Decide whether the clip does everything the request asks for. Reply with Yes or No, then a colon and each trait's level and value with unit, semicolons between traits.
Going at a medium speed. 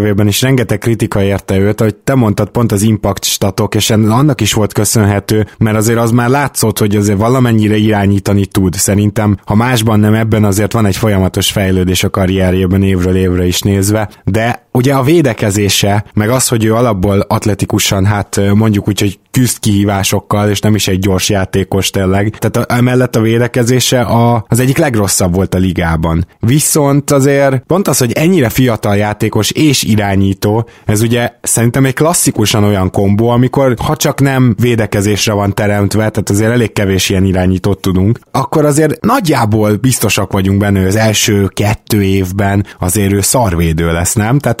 No: fast, 170 wpm